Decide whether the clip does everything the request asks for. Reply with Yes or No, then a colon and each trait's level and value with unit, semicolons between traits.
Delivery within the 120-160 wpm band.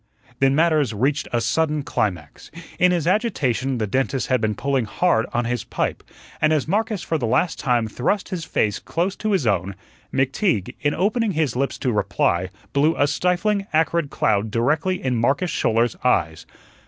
No: average, 175 wpm